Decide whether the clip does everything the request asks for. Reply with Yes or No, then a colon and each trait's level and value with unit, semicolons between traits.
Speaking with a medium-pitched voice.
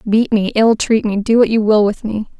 No: high, 215 Hz